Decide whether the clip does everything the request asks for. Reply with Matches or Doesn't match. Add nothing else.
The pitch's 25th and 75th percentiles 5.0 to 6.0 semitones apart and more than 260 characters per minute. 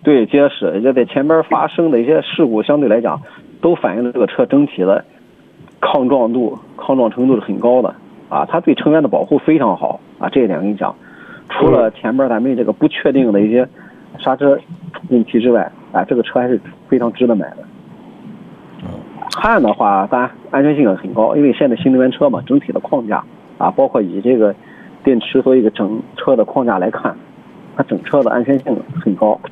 Doesn't match